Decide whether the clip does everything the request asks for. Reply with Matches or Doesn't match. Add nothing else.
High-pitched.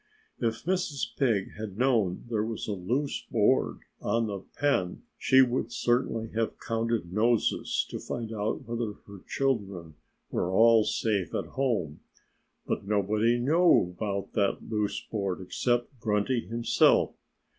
Doesn't match